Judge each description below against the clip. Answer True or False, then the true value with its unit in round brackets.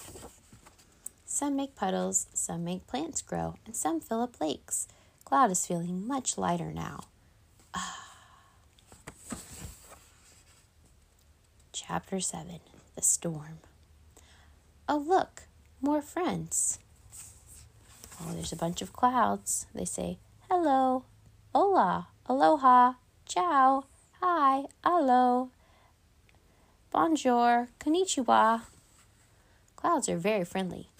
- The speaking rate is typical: False (90 wpm)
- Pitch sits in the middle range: True (165 Hz)